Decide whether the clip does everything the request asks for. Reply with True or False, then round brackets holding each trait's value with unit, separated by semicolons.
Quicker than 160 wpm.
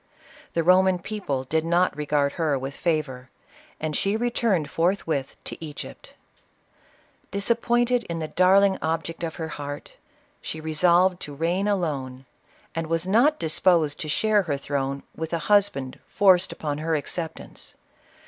False (150 wpm)